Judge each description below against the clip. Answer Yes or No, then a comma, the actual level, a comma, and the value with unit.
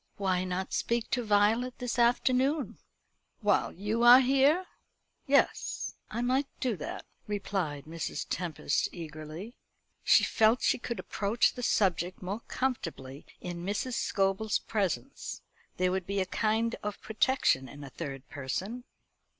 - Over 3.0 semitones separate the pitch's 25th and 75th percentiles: Yes, wide, 5.4 semitones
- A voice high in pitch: Yes, high, 205 Hz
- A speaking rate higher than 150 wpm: No, slow, 135 wpm